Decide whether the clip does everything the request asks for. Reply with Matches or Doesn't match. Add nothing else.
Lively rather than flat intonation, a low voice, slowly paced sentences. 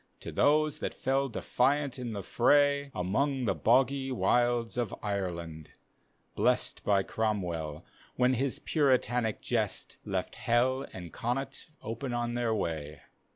Doesn't match